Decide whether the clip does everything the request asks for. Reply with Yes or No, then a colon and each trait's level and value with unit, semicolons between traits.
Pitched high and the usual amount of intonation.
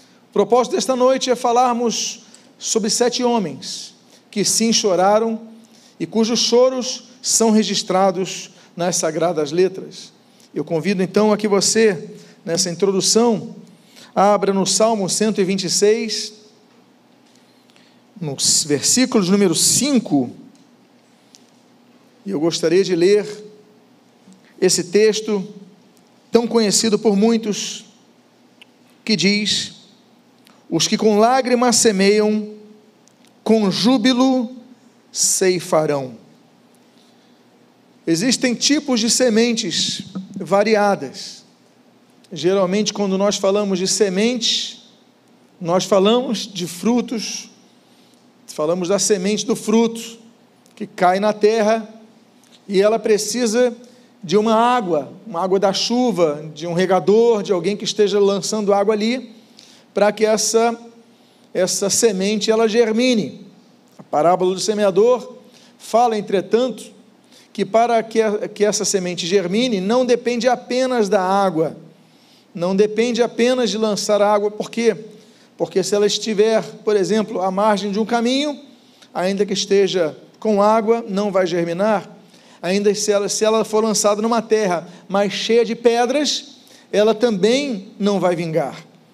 Yes: high, 215 Hz; average, 3.0 semitones